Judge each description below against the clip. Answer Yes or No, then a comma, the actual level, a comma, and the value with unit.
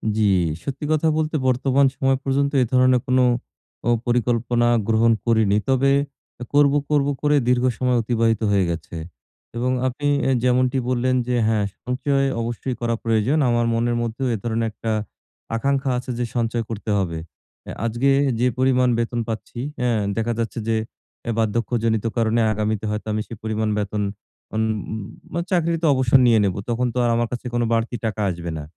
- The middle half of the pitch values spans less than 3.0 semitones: Yes, narrow, 2.4 semitones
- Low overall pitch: Yes, low, 120 Hz